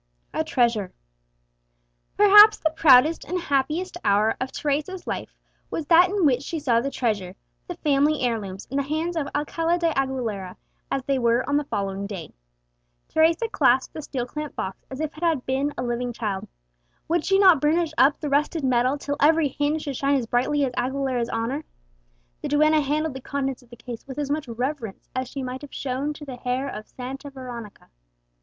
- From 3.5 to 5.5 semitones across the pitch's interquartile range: Yes, average, 3.9 semitones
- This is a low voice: No, very high, 275 Hz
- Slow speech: No, average, 190 wpm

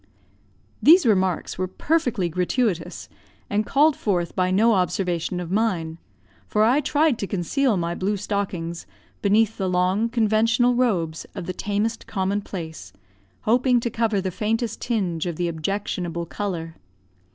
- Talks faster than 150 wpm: No, average, 140 wpm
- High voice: Yes, high, 200 Hz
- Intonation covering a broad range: No, average, 4.3 semitones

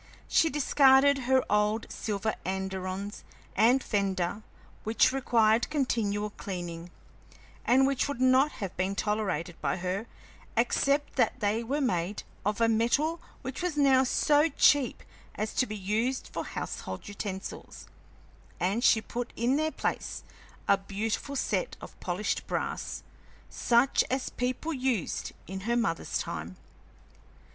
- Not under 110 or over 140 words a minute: Yes, slow, 135 wpm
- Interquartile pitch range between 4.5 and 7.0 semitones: Yes, average, 4.9 semitones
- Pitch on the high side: Yes, high, 230 Hz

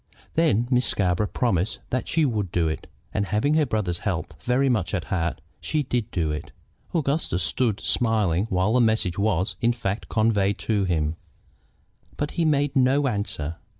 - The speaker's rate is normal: Yes, average, 170 wpm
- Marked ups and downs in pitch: Yes, wide, 5.7 semitones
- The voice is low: Yes, low, 110 Hz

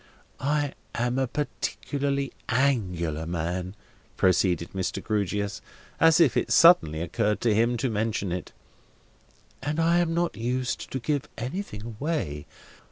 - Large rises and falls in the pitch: Yes, wide, 7.2 semitones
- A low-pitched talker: Yes, low, 120 Hz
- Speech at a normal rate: No, slow, 130 wpm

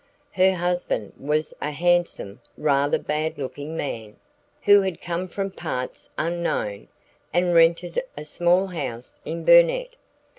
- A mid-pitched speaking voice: Yes, medium, 170 Hz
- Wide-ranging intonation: No, average, 3.7 semitones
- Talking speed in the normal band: No, slow, 125 wpm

